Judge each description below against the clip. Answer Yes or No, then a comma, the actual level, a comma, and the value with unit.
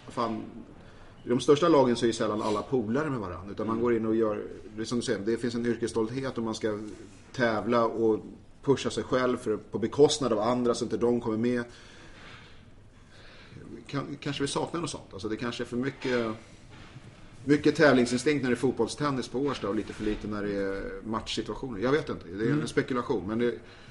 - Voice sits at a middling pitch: No, low, 115 Hz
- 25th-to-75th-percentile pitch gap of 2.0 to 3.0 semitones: Yes, narrow, 2.4 semitones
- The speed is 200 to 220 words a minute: Yes, fast, 205 wpm